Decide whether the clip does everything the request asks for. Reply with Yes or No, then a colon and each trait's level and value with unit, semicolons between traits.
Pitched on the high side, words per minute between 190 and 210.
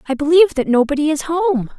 Yes: very high, 300 Hz; average, 200 wpm